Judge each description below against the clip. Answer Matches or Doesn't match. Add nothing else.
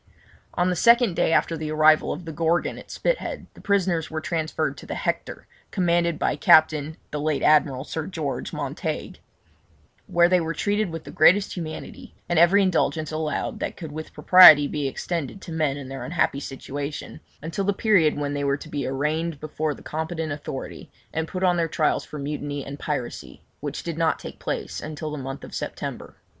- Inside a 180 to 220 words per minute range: Matches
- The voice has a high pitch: Doesn't match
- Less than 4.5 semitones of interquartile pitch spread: Matches